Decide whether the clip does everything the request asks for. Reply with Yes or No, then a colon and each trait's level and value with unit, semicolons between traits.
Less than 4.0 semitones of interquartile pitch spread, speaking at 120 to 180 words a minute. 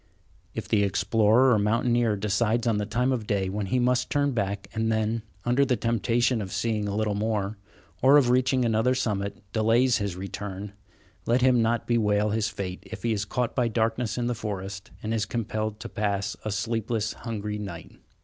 No: narrow, 2.6 semitones; average, 190 wpm